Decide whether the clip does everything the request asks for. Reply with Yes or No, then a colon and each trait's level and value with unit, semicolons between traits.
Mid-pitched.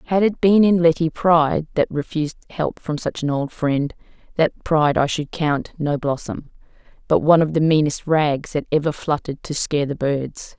Yes: medium, 155 Hz